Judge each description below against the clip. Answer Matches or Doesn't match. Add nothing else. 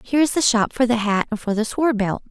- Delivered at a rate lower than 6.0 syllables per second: Doesn't match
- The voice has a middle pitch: Doesn't match